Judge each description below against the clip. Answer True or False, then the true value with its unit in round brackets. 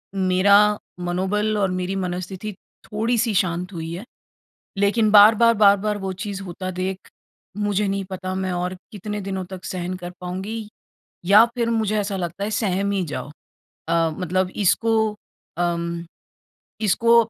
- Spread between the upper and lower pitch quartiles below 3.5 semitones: True (2.4 semitones)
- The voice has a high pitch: True (195 Hz)